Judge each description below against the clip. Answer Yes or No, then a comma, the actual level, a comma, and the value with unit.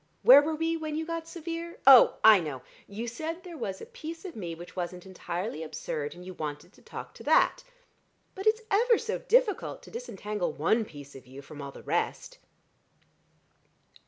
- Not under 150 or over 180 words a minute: No, average, 190 wpm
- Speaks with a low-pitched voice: No, high, 230 Hz